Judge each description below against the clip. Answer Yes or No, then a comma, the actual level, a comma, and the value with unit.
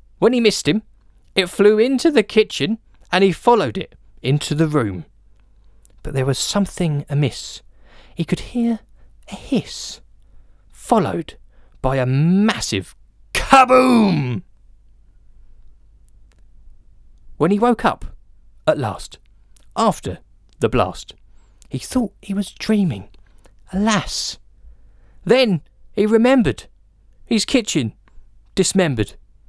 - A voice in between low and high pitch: Yes, medium, 145 Hz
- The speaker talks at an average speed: No, slow, 105 wpm